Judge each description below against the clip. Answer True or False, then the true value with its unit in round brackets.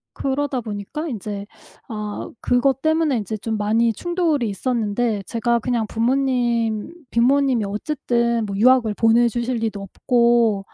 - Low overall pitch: False (235 Hz)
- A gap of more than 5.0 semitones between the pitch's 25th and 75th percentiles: False (3.1 semitones)